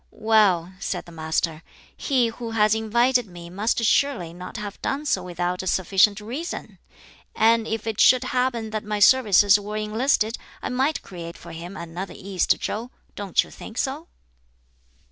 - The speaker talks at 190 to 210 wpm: No, average, 165 wpm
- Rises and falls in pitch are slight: No, average, 4.5 semitones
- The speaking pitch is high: Yes, high, 210 Hz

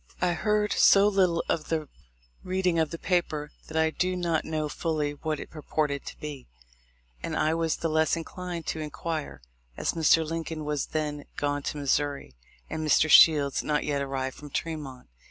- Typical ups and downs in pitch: No, narrow, 2.1 semitones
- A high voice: No, medium, 155 Hz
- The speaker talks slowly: No, average, 175 wpm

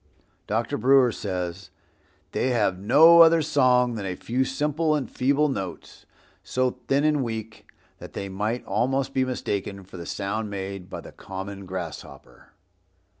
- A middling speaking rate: Yes, average, 150 wpm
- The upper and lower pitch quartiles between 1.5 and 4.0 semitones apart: No, wide, 5.5 semitones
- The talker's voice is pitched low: Yes, low, 115 Hz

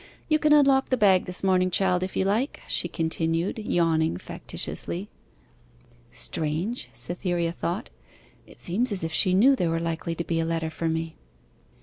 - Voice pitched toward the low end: No, medium, 175 Hz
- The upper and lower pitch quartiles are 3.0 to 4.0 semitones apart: Yes, average, 3.6 semitones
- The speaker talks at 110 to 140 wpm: No, average, 165 wpm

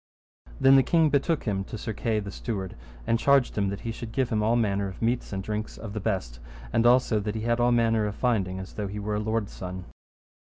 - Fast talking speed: Yes, fast, 250 wpm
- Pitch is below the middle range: Yes, low, 110 Hz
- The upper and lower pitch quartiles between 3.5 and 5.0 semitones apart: No, average, 2.9 semitones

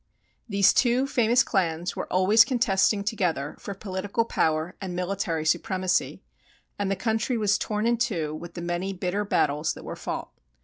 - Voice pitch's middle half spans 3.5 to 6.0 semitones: Yes, average, 4.0 semitones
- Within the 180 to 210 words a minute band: No, average, 165 wpm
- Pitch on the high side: Yes, high, 195 Hz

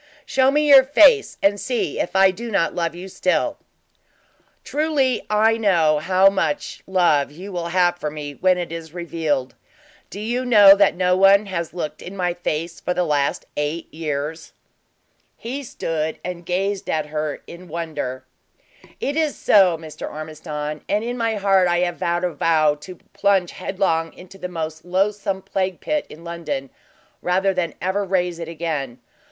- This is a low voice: No, medium, 180 Hz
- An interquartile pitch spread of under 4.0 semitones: Yes, average, 3.6 semitones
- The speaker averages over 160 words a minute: Yes, average, 170 wpm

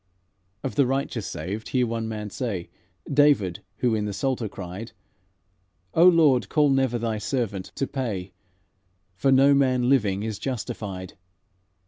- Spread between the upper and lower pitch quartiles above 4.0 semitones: Yes, average, 4.7 semitones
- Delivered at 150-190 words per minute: No, average, 140 wpm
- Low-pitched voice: Yes, low, 115 Hz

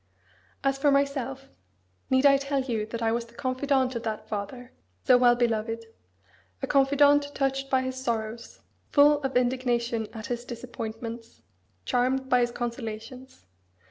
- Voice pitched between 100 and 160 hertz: No, very high, 250 Hz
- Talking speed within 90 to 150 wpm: Yes, average, 145 wpm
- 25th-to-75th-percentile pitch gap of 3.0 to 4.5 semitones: No, narrow, 2.6 semitones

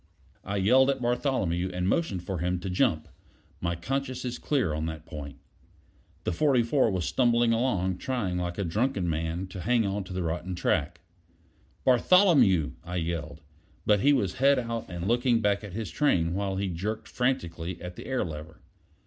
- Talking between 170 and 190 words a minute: Yes, average, 175 wpm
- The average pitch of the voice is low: Yes, very low, 95 Hz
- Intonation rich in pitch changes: Yes, wide, 5.9 semitones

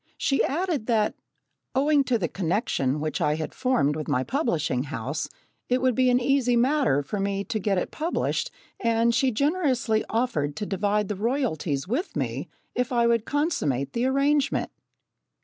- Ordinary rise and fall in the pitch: No, wide, 8.3 semitones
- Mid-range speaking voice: No, high, 230 Hz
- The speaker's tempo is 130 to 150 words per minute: No, average, 165 wpm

